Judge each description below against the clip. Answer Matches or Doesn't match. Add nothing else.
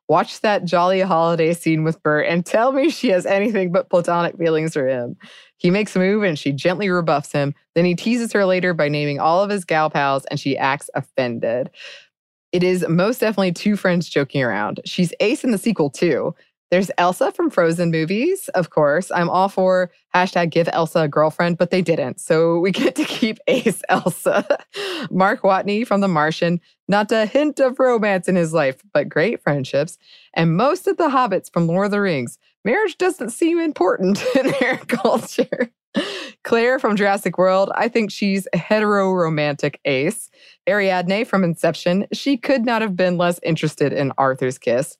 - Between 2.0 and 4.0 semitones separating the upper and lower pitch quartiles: Doesn't match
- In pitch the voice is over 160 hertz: Matches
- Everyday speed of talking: Matches